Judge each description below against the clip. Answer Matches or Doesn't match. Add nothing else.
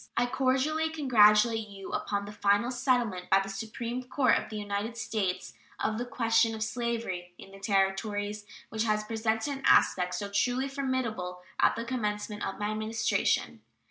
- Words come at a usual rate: Matches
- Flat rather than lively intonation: Doesn't match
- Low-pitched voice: Doesn't match